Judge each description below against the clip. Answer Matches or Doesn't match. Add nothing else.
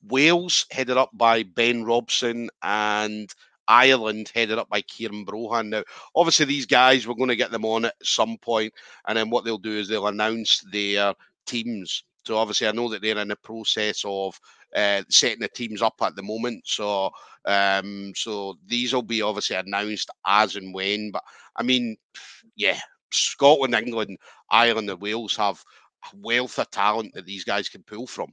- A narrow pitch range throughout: Matches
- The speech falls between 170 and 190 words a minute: Matches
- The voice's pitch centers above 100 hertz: Matches